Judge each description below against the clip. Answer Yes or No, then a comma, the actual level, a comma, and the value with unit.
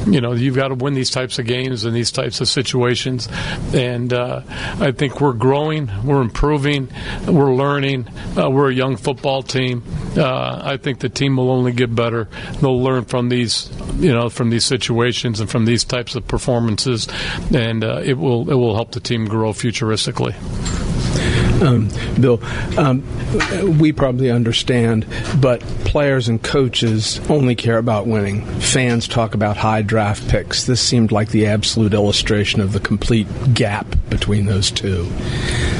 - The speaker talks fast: No, average, 165 wpm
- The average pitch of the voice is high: No, low, 120 Hz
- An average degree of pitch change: Yes, average, 3.1 semitones